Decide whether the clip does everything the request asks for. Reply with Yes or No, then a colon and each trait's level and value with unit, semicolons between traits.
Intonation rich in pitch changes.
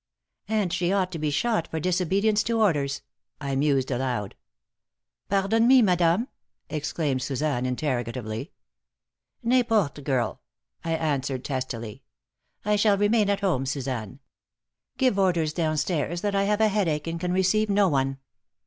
Yes: wide, 6.8 semitones